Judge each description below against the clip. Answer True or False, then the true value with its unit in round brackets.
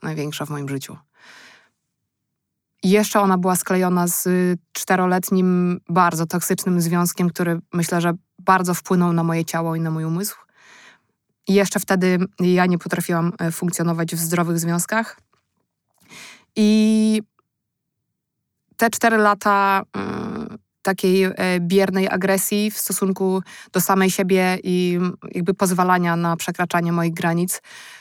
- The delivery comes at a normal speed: True (120 wpm)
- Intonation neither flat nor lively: False (2.0 semitones)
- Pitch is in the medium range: True (180 Hz)